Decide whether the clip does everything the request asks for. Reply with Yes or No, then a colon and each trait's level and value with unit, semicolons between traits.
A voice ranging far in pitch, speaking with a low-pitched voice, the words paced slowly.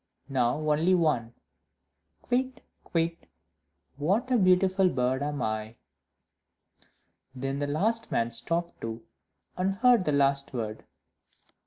No: wide, 6.6 semitones; medium, 150 Hz; slow, 115 wpm